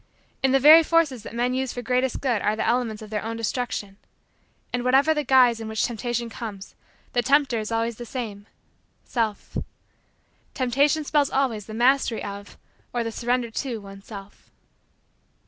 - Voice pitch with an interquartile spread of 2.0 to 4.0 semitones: Yes, average, 3.2 semitones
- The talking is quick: No, average, 170 wpm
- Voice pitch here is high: Yes, high, 240 Hz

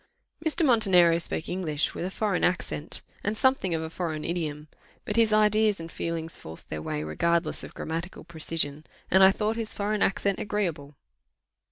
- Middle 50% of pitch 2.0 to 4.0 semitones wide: No, average, 4.6 semitones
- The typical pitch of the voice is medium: Yes, medium, 175 Hz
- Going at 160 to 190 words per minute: Yes, average, 170 wpm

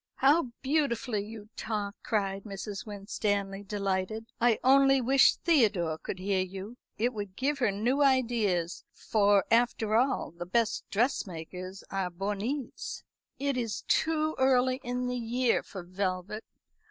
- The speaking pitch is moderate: No, high, 215 Hz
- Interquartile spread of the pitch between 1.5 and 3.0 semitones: No, average, 4.4 semitones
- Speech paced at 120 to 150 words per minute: Yes, slow, 135 wpm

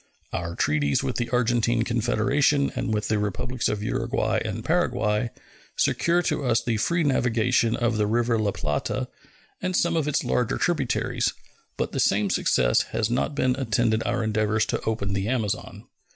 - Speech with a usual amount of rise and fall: Yes, average, 3.0 semitones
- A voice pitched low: Yes, low, 115 Hz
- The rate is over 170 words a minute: No, average, 165 wpm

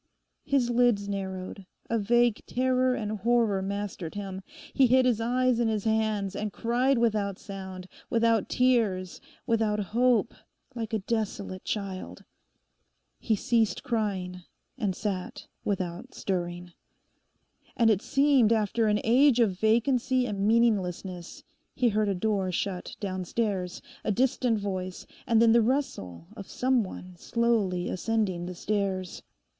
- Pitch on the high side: Yes, high, 215 Hz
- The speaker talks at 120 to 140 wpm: Yes, slow, 135 wpm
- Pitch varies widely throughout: No, average, 3.7 semitones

